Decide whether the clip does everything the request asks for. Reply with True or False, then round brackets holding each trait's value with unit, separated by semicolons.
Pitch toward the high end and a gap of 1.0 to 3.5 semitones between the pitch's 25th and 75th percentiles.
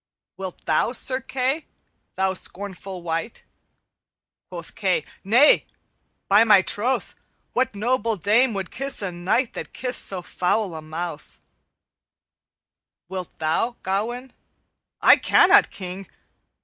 False (200 Hz; 5.3 semitones)